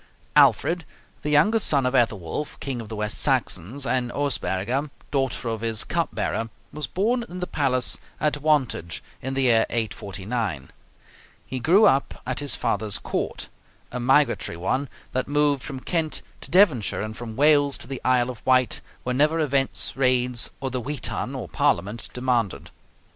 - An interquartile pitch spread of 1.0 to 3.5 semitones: No, average, 4.0 semitones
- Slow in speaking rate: No, average, 160 wpm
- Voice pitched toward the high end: No, low, 130 Hz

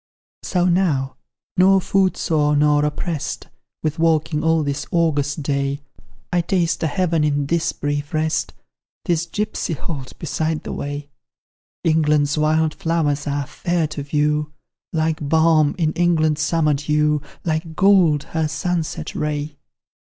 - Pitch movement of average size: No, narrow, 2.1 semitones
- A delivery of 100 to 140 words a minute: Yes, slow, 135 wpm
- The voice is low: No, medium, 155 Hz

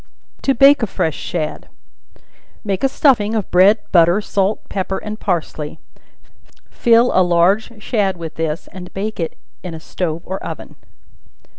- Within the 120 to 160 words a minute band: Yes, average, 150 wpm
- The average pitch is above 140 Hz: Yes, high, 190 Hz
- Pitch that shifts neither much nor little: Yes, average, 4.0 semitones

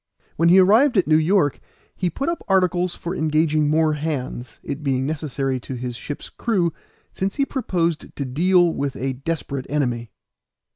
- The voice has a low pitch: No, medium, 155 Hz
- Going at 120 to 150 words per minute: No, average, 165 wpm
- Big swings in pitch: No, average, 4.8 semitones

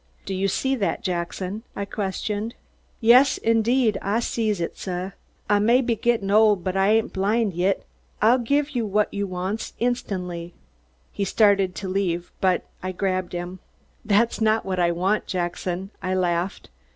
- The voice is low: No, high, 200 Hz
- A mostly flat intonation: No, average, 3.3 semitones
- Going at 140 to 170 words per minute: Yes, average, 165 wpm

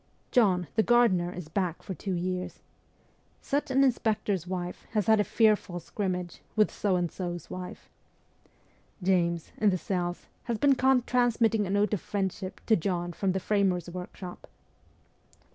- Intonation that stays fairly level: No, average, 3.3 semitones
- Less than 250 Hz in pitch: Yes, high, 190 Hz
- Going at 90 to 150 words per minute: No, average, 165 wpm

